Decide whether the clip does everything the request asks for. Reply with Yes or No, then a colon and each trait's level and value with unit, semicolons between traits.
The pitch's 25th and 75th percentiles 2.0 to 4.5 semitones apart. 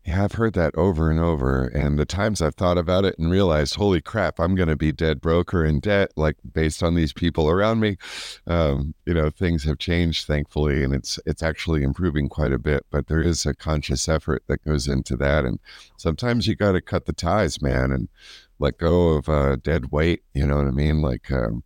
Yes: average, 3.2 semitones